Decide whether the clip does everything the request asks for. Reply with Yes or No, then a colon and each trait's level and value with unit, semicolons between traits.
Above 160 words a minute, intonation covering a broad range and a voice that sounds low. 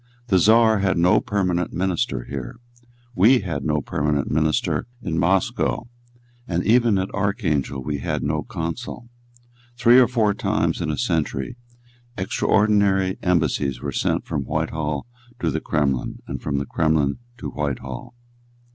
No: average, 140 wpm; wide, 5.7 semitones; very low, 85 Hz